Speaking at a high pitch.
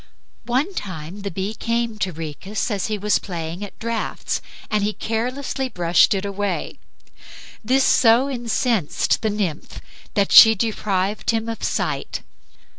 Yes: high, 210 Hz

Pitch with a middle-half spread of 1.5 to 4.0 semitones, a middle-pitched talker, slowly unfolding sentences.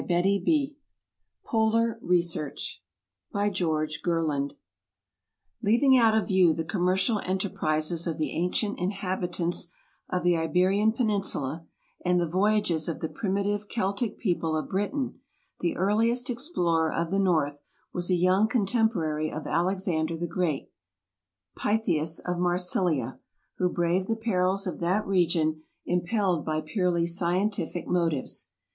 Yes: average, 3.7 semitones; medium, 180 Hz; slow, 125 wpm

